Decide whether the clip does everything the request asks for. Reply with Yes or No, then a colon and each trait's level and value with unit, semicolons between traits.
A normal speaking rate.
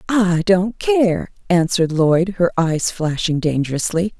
No: slow, 130 wpm